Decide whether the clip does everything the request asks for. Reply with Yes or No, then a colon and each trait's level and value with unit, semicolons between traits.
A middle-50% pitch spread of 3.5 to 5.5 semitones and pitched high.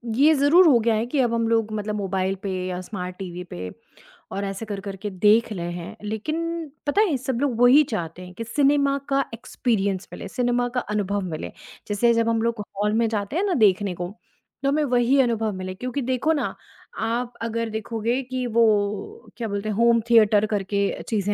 Yes: average, 3.8 semitones; high, 225 Hz